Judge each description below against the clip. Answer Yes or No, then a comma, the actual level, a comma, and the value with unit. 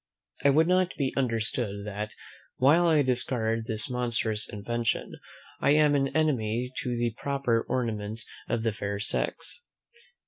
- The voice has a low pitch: Yes, low, 120 Hz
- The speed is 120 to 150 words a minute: Yes, average, 140 wpm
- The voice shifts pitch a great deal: No, average, 3.9 semitones